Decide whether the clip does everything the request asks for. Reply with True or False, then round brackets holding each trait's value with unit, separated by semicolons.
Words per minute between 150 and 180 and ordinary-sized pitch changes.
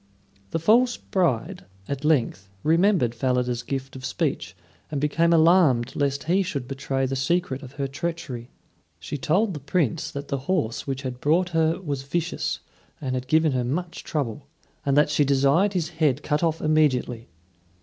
True (170 wpm; 4.0 semitones)